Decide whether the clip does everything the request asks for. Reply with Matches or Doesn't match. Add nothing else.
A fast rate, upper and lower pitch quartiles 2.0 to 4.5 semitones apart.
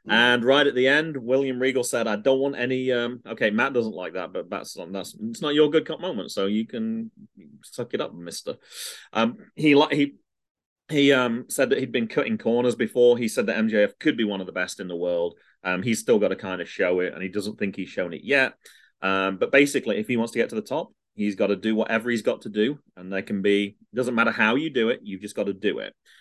Doesn't match